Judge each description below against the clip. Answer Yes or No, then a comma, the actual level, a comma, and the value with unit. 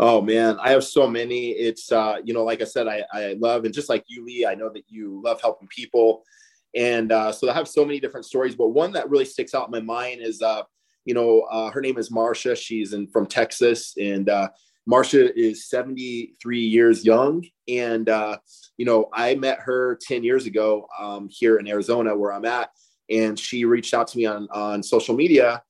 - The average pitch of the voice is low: Yes, low, 115 Hz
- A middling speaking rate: No, fast, 215 wpm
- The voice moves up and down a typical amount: No, narrow, 1.9 semitones